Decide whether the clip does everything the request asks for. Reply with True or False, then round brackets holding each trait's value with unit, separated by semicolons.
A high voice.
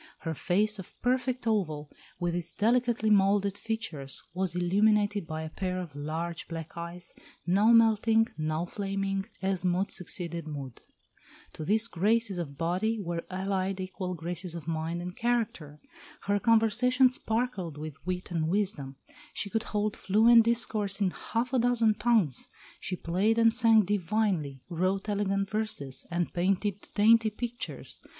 True (195 Hz)